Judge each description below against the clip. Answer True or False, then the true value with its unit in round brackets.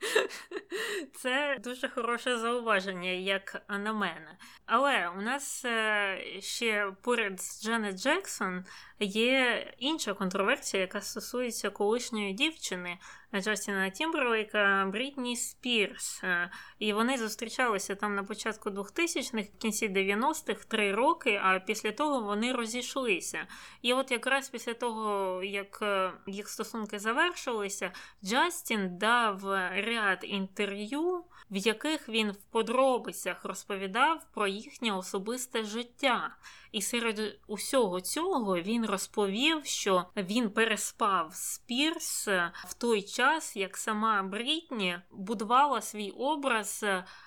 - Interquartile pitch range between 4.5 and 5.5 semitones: False (4.1 semitones)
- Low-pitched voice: False (220 Hz)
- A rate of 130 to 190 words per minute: False (110 wpm)